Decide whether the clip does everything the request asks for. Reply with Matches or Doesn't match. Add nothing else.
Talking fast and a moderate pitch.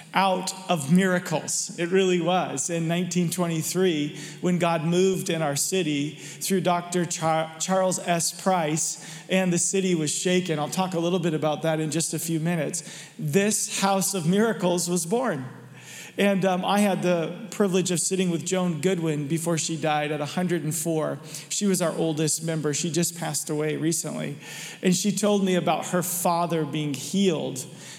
Doesn't match